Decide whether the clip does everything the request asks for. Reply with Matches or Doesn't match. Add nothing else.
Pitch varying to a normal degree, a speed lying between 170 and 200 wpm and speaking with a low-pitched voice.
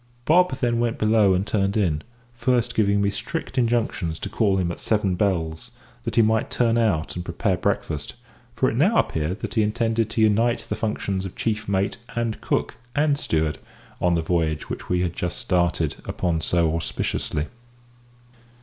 Matches